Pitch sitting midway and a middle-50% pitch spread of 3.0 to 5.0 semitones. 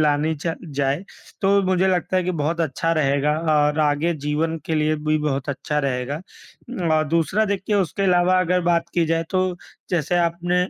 Yes: medium, 165 Hz; average, 3.3 semitones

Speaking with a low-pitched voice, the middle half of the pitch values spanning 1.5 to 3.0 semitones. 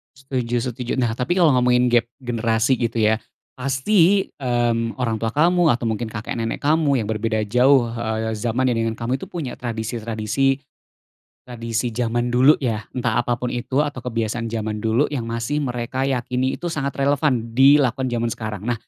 Yes: low, 120 Hz; average, 2.7 semitones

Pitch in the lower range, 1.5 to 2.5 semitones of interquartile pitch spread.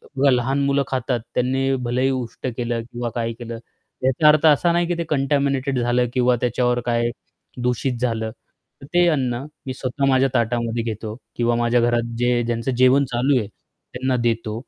Yes: low, 125 Hz; narrow, 2.2 semitones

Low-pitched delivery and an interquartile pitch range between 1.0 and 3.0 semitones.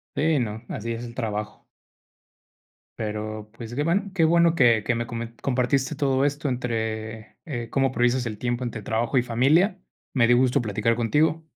No: low, 120 Hz; average, 3.5 semitones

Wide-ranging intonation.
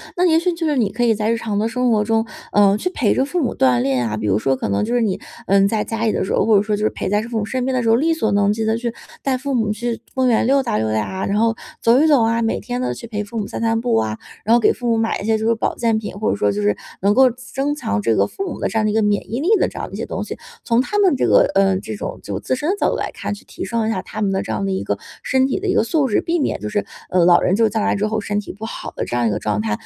No: average, 3.8 semitones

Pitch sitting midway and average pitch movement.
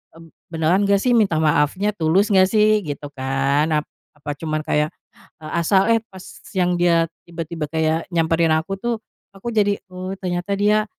Yes: medium, 175 Hz; average, 4.1 semitones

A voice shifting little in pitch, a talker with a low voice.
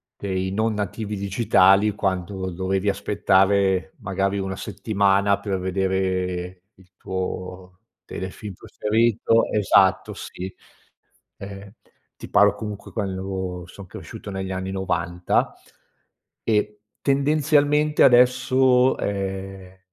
Yes: narrow, 2.0 semitones; very low, 95 Hz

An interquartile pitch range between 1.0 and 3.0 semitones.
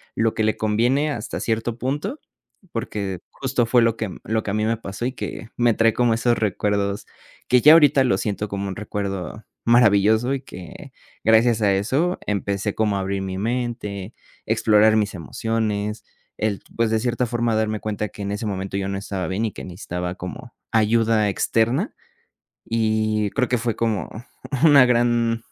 Yes: average, 2.7 semitones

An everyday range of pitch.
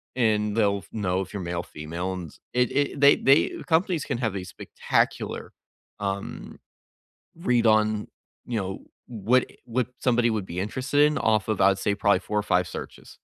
Yes: average, 4.3 semitones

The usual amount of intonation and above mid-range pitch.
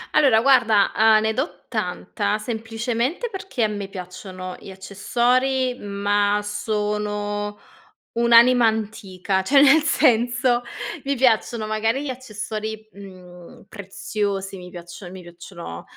Yes: average, 3.3 semitones; high, 215 Hz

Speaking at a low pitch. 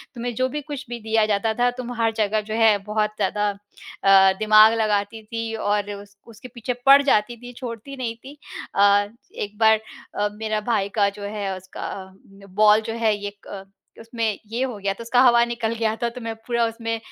No: high, 220 Hz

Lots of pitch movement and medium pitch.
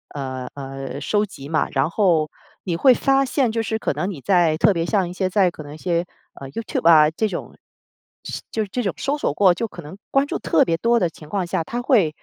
Yes: wide, 5.9 semitones; medium, 180 Hz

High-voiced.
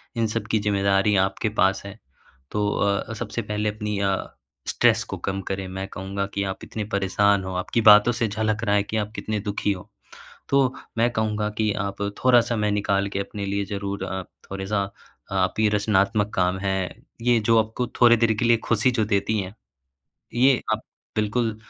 No: low, 105 Hz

